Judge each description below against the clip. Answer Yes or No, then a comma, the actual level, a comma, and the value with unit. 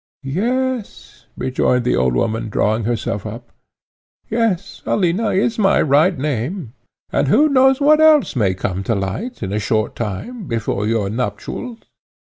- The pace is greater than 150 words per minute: No, average, 145 wpm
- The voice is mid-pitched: No, low, 130 Hz